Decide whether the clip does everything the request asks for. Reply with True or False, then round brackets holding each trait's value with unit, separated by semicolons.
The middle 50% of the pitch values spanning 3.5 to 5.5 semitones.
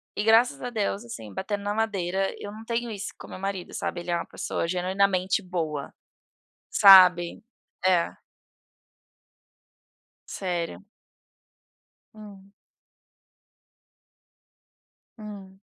False (2.8 semitones)